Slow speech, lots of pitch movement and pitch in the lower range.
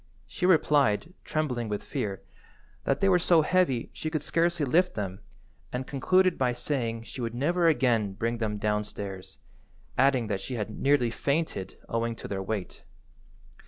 No: average, 160 wpm; wide, 6.4 semitones; low, 125 Hz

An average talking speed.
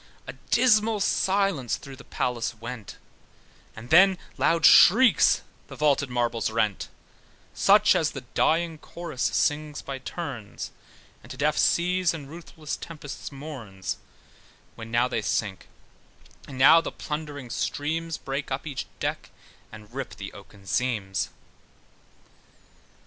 No: slow, 125 wpm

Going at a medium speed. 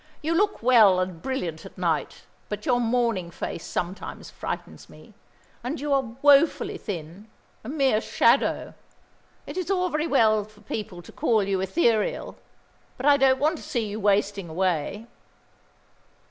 Yes: average, 155 wpm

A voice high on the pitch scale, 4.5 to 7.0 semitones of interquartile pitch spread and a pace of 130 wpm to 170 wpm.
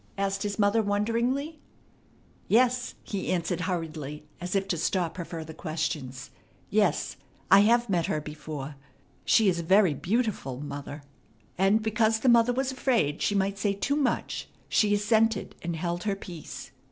Yes: high, 195 Hz; average, 5.2 semitones; average, 155 wpm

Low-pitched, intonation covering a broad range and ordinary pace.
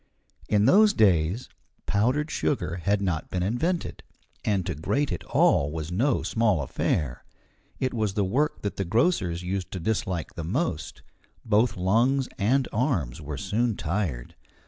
Yes: low, 100 Hz; wide, 6.2 semitones; average, 150 wpm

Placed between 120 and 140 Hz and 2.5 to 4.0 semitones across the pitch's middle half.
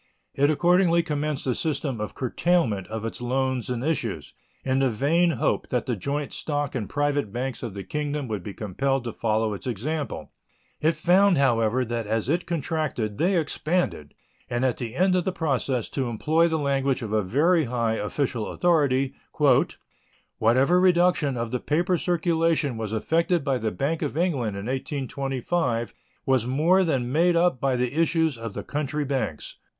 No: low, 135 Hz; wide, 5.4 semitones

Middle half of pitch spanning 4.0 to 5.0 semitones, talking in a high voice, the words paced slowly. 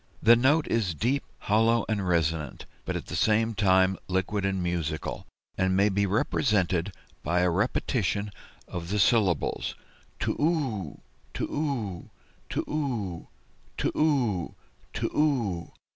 No: average, 4.5 semitones; low, 100 Hz; slow, 130 wpm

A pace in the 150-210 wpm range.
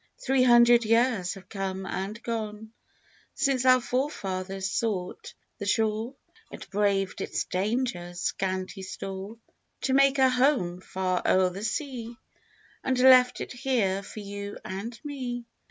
No: average, 140 wpm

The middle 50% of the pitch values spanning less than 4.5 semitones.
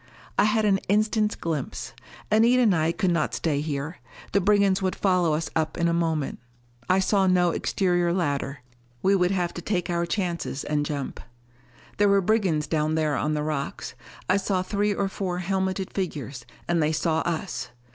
Yes: average, 3.9 semitones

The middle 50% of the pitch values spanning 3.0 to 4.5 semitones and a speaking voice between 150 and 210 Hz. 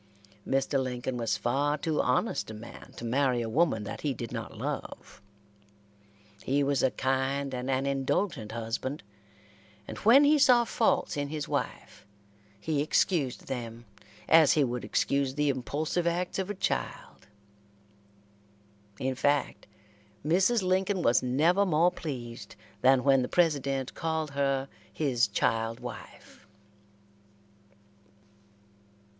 No: average, 4.2 semitones; medium, 140 Hz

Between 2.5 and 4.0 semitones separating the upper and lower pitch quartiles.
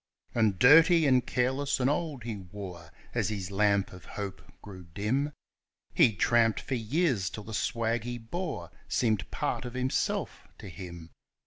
No: average, 4.6 semitones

